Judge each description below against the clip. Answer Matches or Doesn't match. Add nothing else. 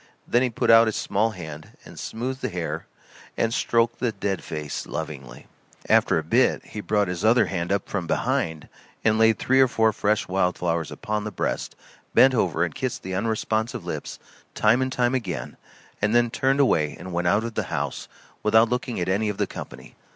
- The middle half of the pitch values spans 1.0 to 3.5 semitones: Doesn't match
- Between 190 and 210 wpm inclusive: Matches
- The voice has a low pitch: Matches